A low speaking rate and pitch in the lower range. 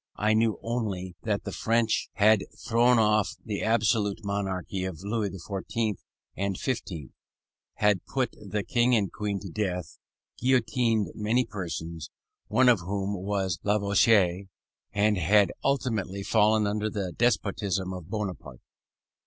Yes: slow, 130 wpm; low, 105 Hz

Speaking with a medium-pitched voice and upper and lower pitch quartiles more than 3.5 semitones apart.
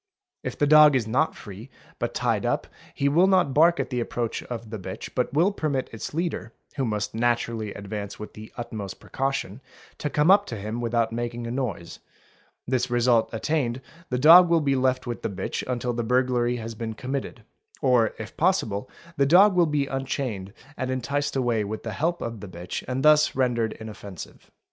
No: low, 125 Hz; average, 4.1 semitones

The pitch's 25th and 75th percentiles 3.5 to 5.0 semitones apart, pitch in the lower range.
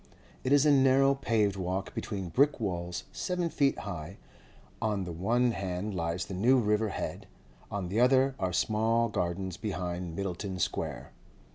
No: wide, 5.4 semitones; low, 100 Hz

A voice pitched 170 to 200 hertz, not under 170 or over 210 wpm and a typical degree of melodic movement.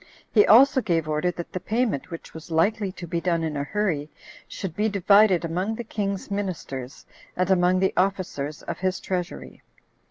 Yes: medium, 185 Hz; average, 180 wpm; average, 3.6 semitones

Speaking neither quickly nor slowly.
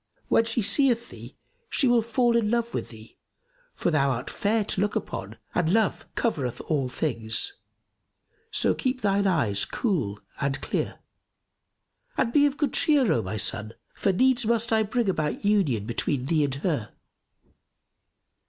Yes: average, 160 wpm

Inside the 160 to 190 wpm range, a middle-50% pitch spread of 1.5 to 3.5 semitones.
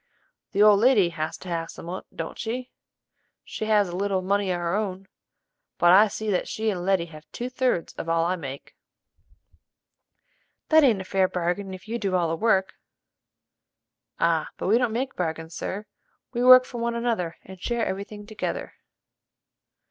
No: average, 180 wpm; average, 4.1 semitones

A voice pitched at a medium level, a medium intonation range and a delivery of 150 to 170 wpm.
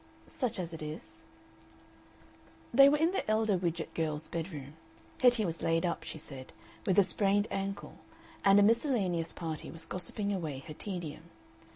Yes: medium, 180 Hz; average, 4.2 semitones; average, 160 wpm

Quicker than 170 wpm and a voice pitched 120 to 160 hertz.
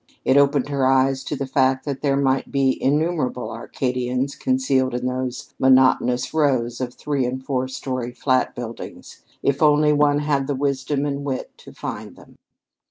No: average, 165 wpm; low, 135 Hz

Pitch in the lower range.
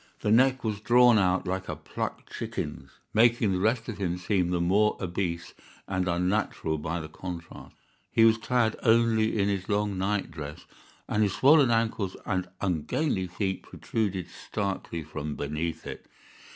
Yes: very low, 95 Hz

